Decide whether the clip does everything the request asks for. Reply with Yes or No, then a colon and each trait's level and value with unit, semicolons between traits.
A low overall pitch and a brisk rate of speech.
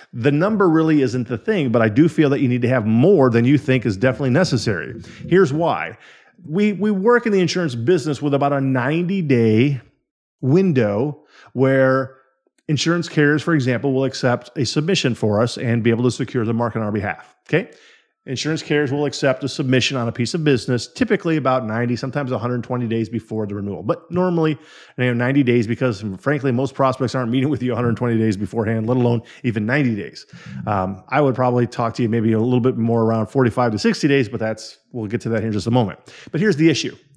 Yes: low, 130 Hz; fast, 225 wpm